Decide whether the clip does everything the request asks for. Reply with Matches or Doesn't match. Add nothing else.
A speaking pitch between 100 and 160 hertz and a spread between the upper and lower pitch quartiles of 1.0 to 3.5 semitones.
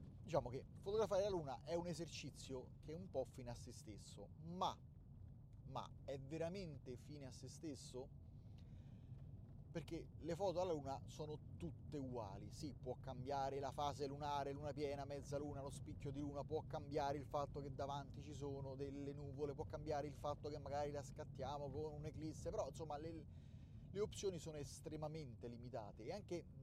Matches